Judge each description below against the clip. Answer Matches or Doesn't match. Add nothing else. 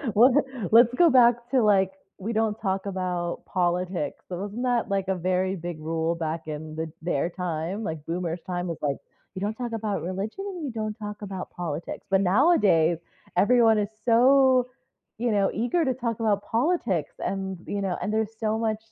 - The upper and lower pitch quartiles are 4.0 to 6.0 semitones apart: Matches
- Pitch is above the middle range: Matches